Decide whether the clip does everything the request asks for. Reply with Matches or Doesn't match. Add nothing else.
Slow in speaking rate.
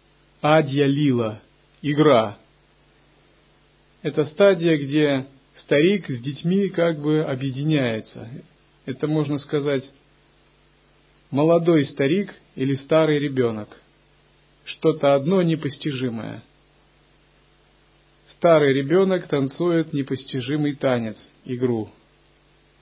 Matches